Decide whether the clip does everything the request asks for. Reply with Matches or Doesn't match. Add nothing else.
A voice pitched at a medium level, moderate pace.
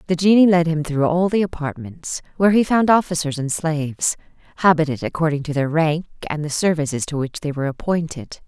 Matches